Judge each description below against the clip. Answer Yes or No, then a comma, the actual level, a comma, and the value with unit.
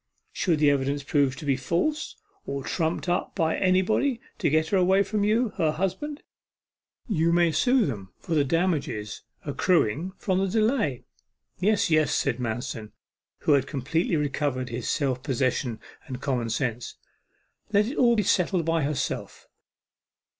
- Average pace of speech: Yes, average, 155 wpm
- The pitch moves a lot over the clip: Yes, wide, 6.0 semitones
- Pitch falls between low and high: Yes, medium, 155 Hz